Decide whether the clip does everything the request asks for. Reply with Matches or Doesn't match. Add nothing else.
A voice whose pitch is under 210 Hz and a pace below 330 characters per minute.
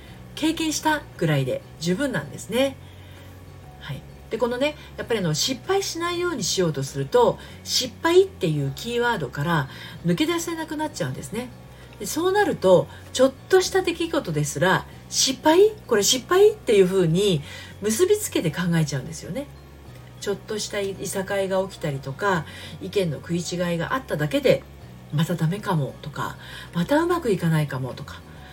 Doesn't match